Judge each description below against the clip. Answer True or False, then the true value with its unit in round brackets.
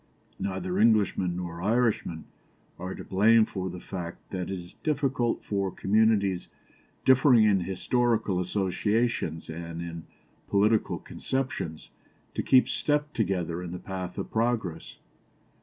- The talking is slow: True (125 wpm)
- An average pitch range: True (4.2 semitones)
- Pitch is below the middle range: True (95 Hz)